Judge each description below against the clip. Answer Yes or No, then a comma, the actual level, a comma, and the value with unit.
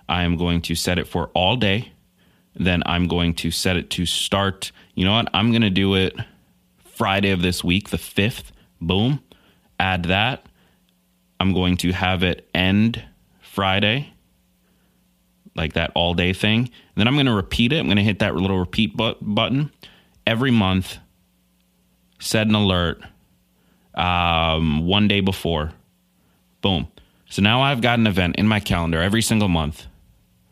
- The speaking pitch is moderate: No, very low, 90 Hz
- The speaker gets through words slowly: No, average, 165 wpm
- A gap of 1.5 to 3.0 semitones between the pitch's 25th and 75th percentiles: No, average, 3.7 semitones